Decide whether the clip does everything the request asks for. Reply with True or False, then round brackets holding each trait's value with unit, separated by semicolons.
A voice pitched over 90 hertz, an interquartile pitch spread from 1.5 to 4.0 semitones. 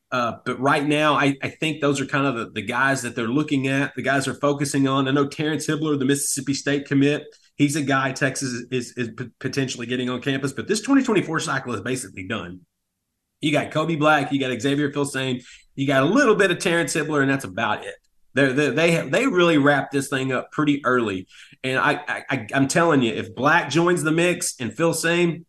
True (140 Hz; 3.0 semitones)